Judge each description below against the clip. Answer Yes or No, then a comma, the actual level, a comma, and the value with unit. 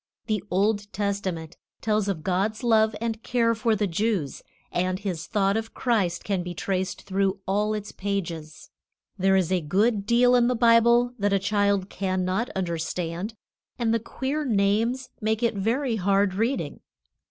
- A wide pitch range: No, average, 3.2 semitones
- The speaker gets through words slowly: No, average, 160 wpm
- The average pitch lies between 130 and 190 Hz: No, high, 205 Hz